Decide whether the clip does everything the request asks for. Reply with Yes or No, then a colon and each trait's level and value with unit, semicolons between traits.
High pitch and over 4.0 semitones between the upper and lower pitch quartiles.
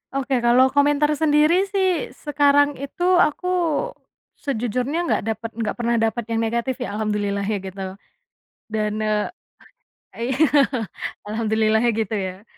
Yes: high, 235 Hz; average, 4.8 semitones